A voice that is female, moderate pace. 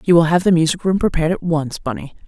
No: female; fast, 265 wpm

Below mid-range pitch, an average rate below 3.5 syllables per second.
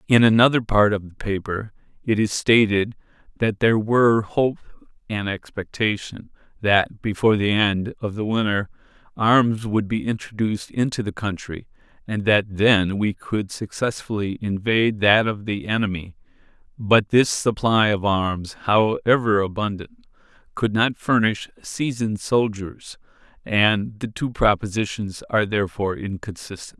No: low, 105 Hz; 4.5 syllables/s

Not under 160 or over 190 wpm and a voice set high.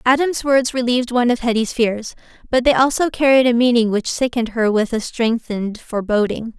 Yes: average, 180 wpm; high, 235 Hz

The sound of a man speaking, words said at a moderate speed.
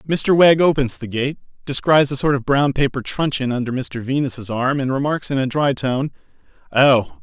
Yes: male; average, 190 wpm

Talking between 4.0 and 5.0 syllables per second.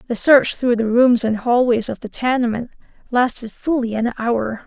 Yes: 4.7 syllables/s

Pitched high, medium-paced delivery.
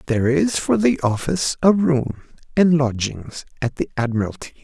No: medium, 145 Hz; average, 155 wpm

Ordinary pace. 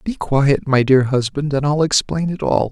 No: fast, 220 wpm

